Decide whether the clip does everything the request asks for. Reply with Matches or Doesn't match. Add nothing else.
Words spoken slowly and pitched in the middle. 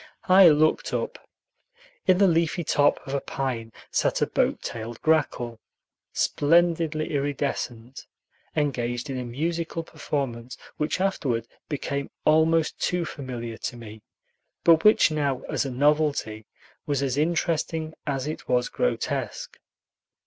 Matches